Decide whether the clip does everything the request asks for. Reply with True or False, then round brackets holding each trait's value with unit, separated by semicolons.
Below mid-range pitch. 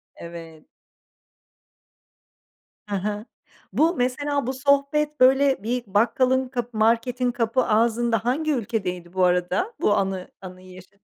False (235 Hz)